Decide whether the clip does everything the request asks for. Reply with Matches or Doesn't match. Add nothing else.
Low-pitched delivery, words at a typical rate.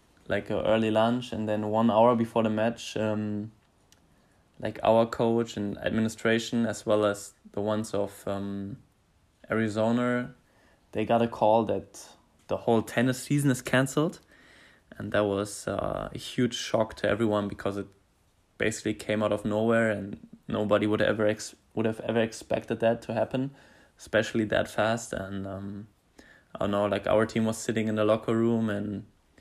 Matches